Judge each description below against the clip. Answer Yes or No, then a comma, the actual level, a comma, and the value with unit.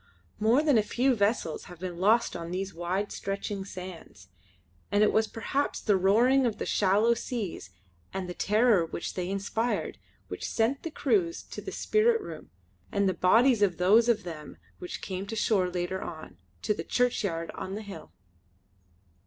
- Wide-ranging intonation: No, average, 4.3 semitones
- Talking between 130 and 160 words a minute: No, average, 175 wpm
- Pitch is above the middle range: Yes, high, 200 Hz